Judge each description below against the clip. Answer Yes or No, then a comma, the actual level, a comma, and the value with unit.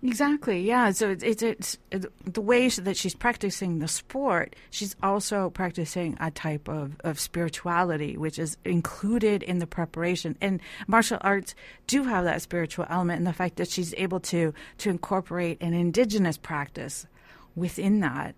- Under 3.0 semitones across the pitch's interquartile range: No, average, 3.3 semitones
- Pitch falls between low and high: Yes, medium, 180 Hz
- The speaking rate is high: No, average, 160 wpm